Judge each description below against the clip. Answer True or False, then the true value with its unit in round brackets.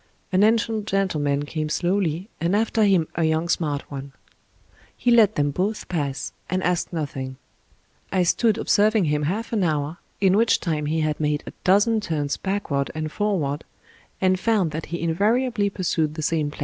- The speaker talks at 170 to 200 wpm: True (175 wpm)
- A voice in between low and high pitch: True (175 Hz)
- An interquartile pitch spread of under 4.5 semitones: False (5.2 semitones)